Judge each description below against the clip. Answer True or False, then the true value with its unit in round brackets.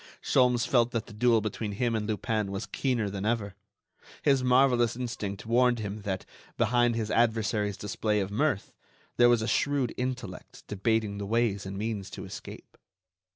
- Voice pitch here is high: False (115 Hz)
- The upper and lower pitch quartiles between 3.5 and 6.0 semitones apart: False (2.9 semitones)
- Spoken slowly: False (165 wpm)